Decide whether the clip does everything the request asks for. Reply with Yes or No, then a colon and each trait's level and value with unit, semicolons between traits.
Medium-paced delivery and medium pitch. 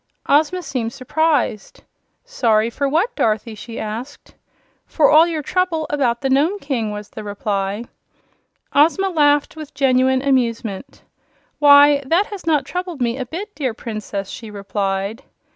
No: average, 145 wpm; very high, 270 Hz